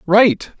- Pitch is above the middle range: Yes, high, 220 Hz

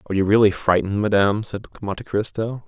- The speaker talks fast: No, average, 180 wpm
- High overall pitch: No, low, 105 Hz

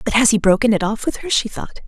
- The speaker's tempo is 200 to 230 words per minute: No, fast, 320 wpm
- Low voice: No, high, 225 Hz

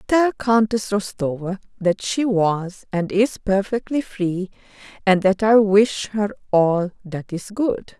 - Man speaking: No, female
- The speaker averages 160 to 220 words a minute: No, average, 145 wpm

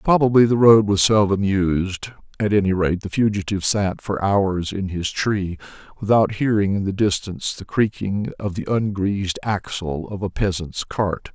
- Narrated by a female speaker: No, male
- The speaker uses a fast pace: No, average, 170 wpm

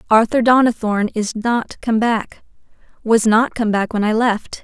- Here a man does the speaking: No, female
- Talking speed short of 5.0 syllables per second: Yes, 4.5 syllables/s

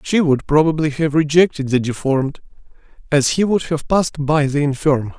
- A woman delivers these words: No, male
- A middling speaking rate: Yes, average, 175 wpm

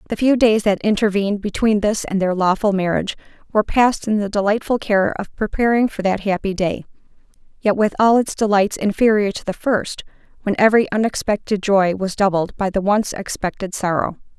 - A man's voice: No, female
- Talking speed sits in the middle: Yes, average, 175 wpm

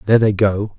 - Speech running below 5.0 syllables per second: No, 6.4 syllables/s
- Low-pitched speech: Yes, low, 105 Hz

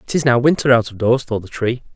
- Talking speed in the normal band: No, fast, 275 wpm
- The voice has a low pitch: Yes, low, 125 Hz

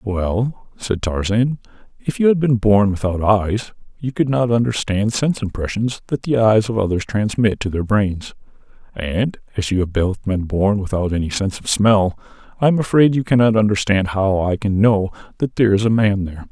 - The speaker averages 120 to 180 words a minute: No, average, 195 wpm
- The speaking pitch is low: Yes, low, 105 Hz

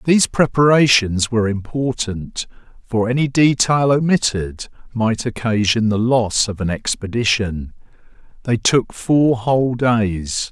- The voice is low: Yes, low, 115 Hz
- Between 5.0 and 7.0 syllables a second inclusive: No, 4.1 syllables/s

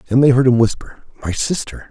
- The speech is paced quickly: Yes, fast, 220 wpm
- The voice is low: Yes, low, 125 Hz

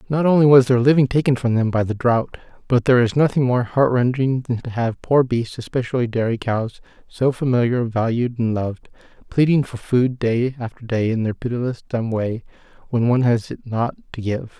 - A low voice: Yes, low, 120 Hz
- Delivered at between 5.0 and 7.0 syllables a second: Yes, 5.3 syllables/s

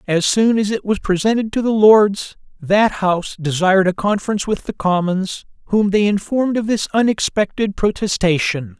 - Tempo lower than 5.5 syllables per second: Yes, 5.1 syllables/s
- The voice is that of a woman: No, male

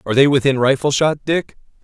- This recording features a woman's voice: No, male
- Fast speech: No, average, 195 wpm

